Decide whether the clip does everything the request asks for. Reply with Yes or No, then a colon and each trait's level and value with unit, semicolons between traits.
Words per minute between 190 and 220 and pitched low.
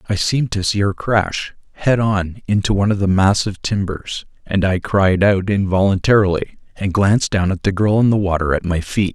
Yes: fast, 205 wpm; low, 100 Hz